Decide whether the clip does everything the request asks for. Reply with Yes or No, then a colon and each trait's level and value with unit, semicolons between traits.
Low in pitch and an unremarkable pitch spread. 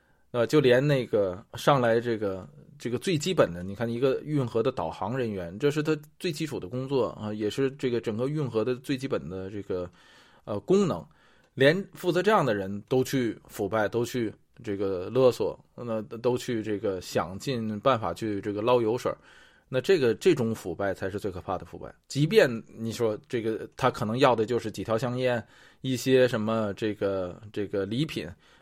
Yes: low, 120 Hz; average, 4.3 semitones